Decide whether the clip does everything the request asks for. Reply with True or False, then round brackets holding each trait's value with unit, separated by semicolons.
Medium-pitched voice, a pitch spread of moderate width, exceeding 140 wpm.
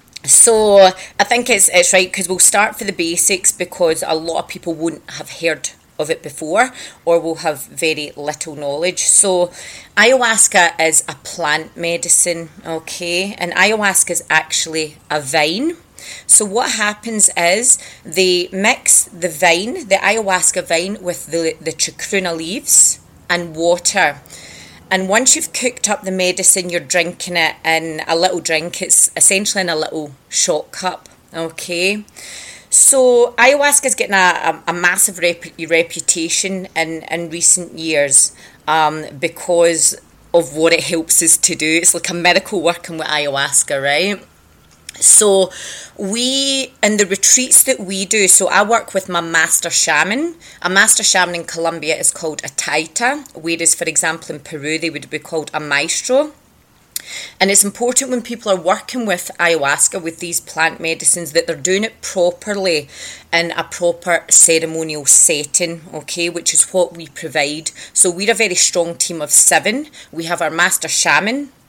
True (175 Hz; 3.2 semitones; 160 wpm)